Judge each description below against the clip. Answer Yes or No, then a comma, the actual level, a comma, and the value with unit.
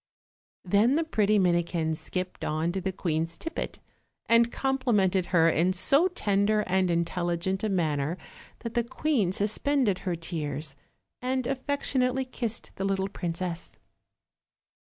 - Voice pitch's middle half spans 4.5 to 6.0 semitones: Yes, wide, 5.6 semitones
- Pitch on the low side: No, high, 190 Hz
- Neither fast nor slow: No, slow, 130 wpm